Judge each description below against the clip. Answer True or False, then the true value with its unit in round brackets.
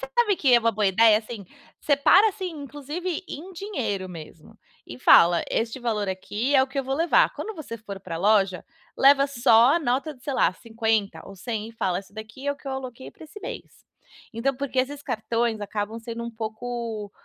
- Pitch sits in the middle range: False (235 Hz)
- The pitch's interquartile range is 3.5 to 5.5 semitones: True (4.6 semitones)